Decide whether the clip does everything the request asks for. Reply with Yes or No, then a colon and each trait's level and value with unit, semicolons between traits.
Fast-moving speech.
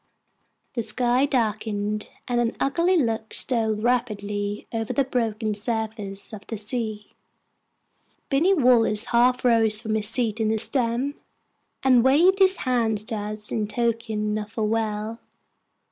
No: slow, 135 wpm